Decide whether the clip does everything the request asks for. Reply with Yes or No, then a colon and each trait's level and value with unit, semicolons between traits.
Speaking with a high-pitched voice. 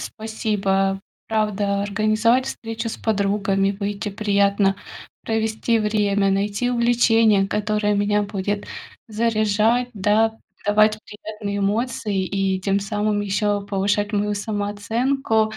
Yes: high, 210 Hz